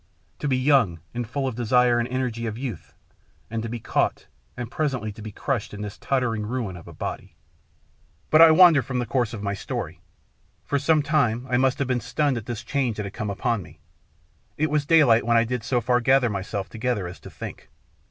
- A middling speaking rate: No, fast, 220 wpm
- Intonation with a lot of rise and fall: No, average, 3.6 semitones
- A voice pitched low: Yes, low, 120 Hz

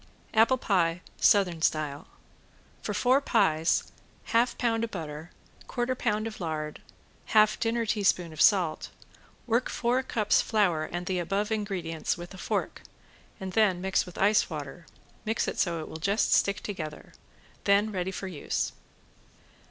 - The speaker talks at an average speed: Yes, average, 150 wpm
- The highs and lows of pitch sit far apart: No, average, 4.8 semitones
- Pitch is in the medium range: No, high, 195 Hz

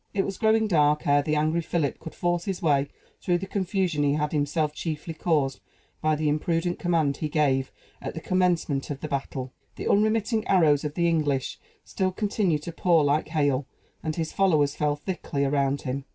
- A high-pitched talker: No, medium, 155 Hz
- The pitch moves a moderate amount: Yes, average, 3.4 semitones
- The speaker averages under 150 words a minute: No, average, 190 wpm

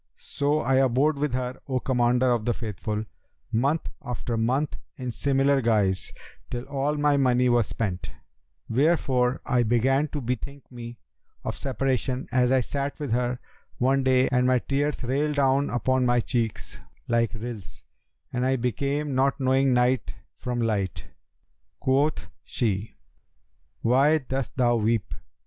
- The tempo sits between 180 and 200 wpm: No, average, 145 wpm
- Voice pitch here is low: Yes, low, 125 Hz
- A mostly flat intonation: Yes, narrow, 2.3 semitones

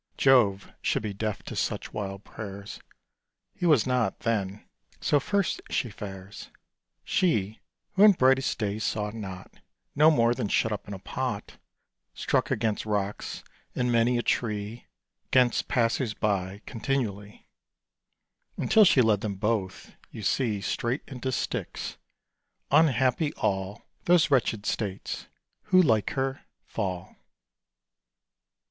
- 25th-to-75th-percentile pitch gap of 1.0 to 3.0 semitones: No, average, 4.3 semitones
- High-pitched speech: No, low, 110 Hz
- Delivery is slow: Yes, slow, 125 wpm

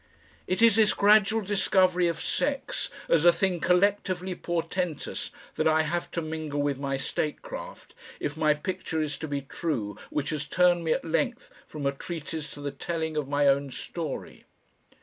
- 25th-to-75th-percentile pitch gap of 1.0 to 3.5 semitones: No, average, 3.9 semitones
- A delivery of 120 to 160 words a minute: No, average, 170 wpm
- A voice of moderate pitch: Yes, medium, 165 Hz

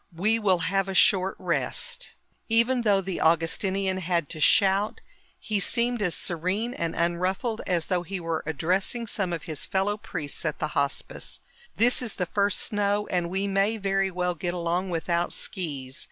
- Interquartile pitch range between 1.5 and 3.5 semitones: Yes, average, 3.1 semitones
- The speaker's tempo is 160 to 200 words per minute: Yes, average, 170 wpm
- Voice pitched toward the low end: No, high, 190 Hz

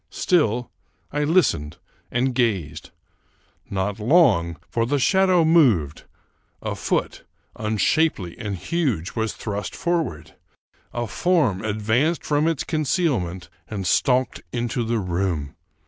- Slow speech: Yes, slow, 115 wpm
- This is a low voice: Yes, low, 115 Hz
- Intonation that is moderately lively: No, wide, 8.3 semitones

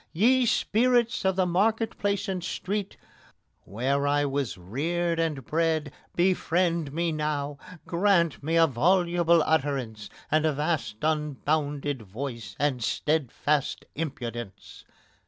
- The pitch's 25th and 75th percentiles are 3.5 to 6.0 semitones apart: Yes, average, 3.9 semitones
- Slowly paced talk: Yes, slow, 120 wpm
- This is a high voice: No, medium, 155 Hz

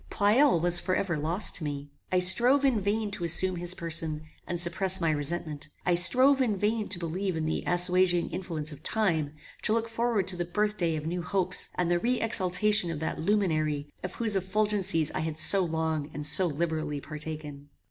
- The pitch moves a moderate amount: Yes, average, 4.3 semitones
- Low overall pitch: No, medium, 175 Hz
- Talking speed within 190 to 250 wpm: Yes, average, 200 wpm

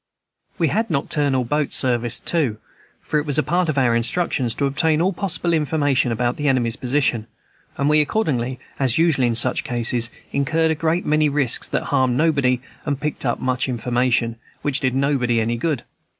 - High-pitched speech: No, low, 135 Hz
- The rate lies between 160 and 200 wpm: Yes, average, 180 wpm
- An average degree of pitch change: Yes, average, 3.9 semitones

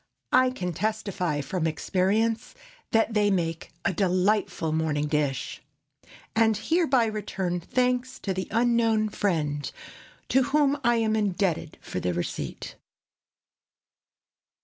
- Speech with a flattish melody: No, average, 5.3 semitones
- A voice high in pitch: Yes, high, 205 Hz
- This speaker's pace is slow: Yes, slow, 115 wpm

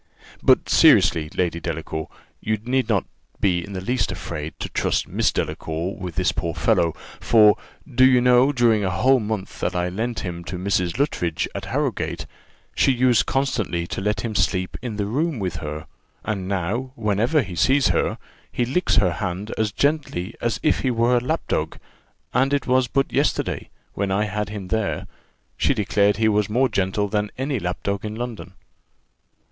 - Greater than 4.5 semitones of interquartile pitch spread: Yes, average, 5.0 semitones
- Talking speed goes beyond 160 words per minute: Yes, average, 180 wpm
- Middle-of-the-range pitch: No, low, 105 Hz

